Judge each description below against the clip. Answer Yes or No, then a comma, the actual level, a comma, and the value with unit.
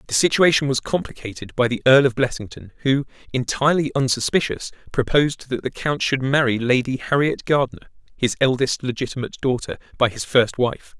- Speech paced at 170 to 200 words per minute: No, average, 160 wpm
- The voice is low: Yes, low, 130 Hz